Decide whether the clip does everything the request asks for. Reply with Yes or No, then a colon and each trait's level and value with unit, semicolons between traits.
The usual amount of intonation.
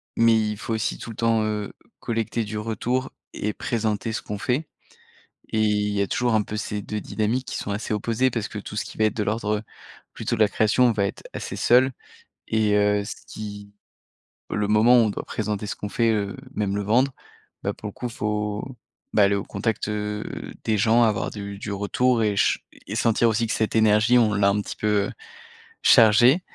No: narrow, 1.7 semitones